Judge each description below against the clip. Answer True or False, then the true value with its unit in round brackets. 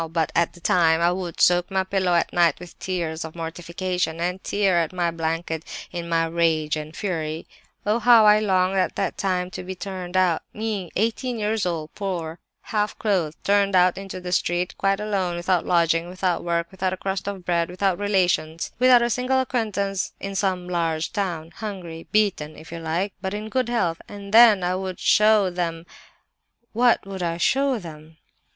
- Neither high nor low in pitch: True (180 Hz)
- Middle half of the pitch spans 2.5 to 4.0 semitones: True (3.0 semitones)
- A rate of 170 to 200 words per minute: True (185 wpm)